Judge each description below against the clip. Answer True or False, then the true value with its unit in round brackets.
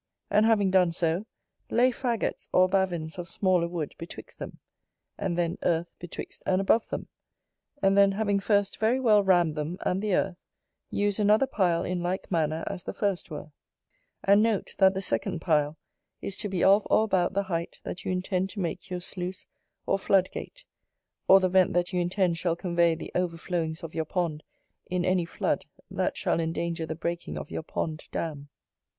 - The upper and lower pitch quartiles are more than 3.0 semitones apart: False (2.6 semitones)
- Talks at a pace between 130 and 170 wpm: False (185 wpm)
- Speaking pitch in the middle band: True (180 Hz)